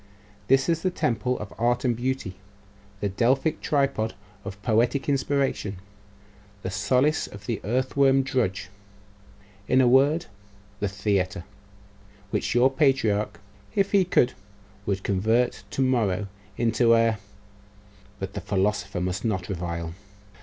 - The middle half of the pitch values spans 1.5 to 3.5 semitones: No, average, 4.9 semitones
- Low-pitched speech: Yes, low, 115 Hz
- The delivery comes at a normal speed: No, slow, 125 wpm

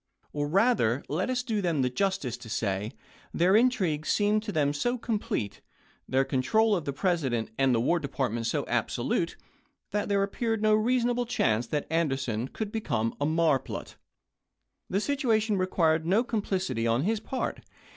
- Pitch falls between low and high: Yes, medium, 175 Hz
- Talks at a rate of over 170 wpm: No, average, 165 wpm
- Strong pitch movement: Yes, wide, 8.3 semitones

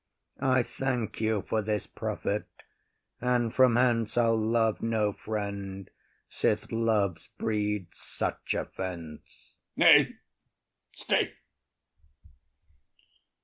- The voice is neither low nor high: No, low, 110 Hz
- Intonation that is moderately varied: No, narrow, 2.3 semitones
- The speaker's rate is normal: No, slow, 95 wpm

